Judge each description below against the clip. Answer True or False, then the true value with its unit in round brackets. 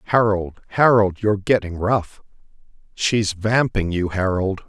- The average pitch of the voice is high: False (100 Hz)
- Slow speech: True (115 wpm)